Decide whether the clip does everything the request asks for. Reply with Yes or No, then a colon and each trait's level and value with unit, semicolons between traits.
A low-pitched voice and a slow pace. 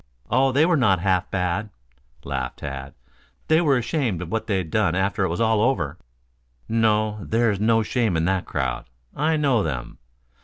No: low, 105 Hz; average, 170 wpm